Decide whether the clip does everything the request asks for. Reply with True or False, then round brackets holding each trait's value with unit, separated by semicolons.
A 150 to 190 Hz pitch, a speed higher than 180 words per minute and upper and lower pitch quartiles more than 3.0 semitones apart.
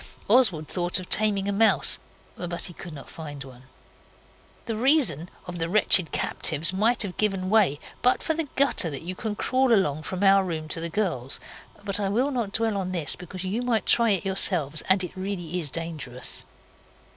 True (185 Hz; 190 wpm; 4.4 semitones)